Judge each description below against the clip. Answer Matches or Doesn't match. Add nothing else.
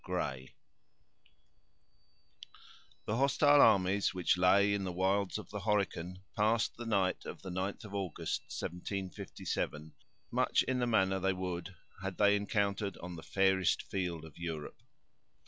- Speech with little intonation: Matches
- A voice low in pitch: Matches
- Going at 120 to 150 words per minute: Matches